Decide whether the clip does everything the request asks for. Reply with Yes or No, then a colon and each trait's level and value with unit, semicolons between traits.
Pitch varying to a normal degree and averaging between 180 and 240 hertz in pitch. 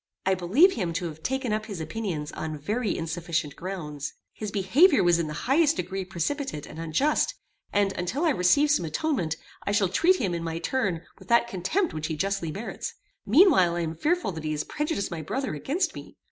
No: wide, 8.2 semitones; high, 190 Hz